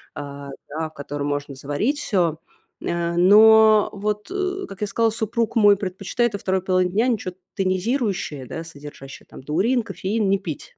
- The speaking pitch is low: No, high, 190 Hz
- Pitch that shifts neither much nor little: No, wide, 5.7 semitones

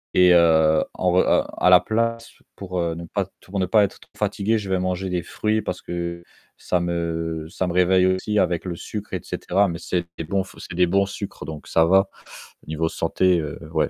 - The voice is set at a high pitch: No, very low, 90 Hz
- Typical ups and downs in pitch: No, narrow, 2.3 semitones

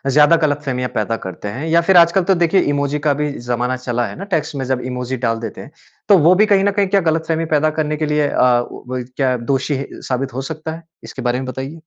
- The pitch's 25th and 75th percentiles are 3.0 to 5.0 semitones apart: Yes, average, 4.3 semitones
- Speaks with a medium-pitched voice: Yes, medium, 145 Hz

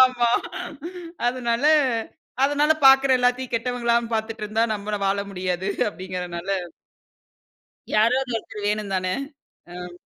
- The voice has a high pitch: Yes, high, 225 Hz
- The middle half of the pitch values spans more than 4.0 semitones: Yes, average, 4.4 semitones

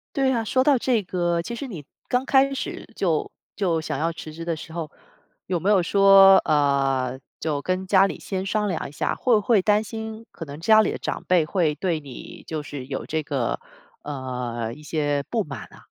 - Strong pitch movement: Yes, wide, 5.9 semitones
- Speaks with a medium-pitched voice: Yes, medium, 175 Hz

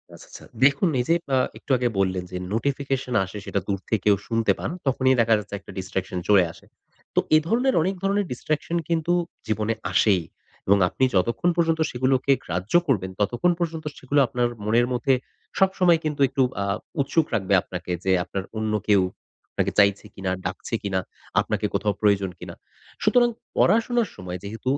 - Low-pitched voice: Yes, low, 120 Hz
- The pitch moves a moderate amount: No, wide, 7.6 semitones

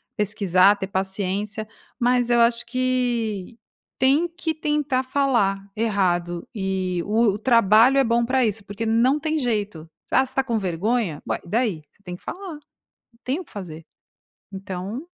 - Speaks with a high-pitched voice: Yes, high, 225 Hz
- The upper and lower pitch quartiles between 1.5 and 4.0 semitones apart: No, average, 4.7 semitones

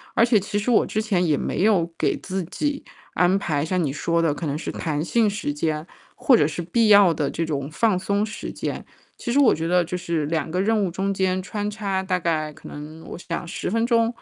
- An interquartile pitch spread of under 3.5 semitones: No, average, 4.4 semitones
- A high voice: No, medium, 180 Hz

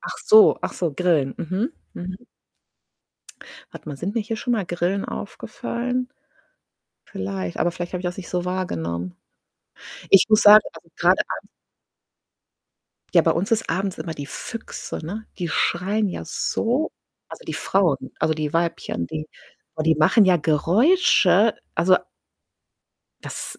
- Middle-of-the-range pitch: Yes, medium, 180 Hz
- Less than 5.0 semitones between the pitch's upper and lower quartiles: No, wide, 5.4 semitones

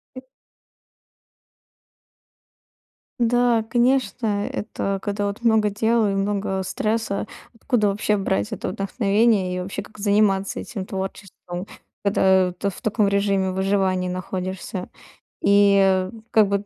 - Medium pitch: No, high, 200 Hz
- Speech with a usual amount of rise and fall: No, narrow, 2.1 semitones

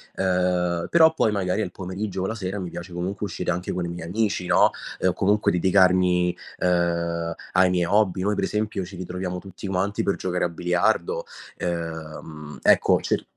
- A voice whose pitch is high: No, very low, 90 Hz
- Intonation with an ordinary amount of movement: No, narrow, 1.8 semitones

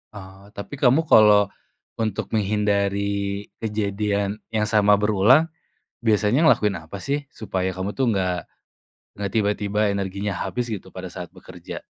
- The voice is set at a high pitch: No, low, 105 Hz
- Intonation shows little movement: Yes, narrow, 1.8 semitones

